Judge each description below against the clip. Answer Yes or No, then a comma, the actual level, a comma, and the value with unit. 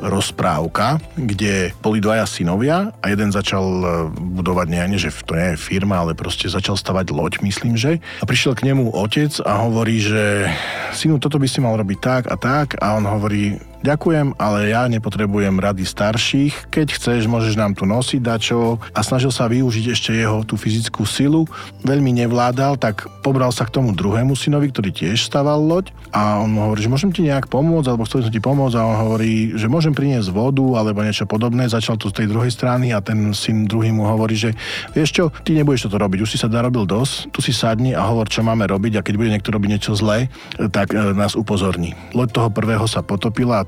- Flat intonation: No, average, 3.8 semitones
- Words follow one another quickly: Yes, fast, 205 wpm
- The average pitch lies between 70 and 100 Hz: No, low, 110 Hz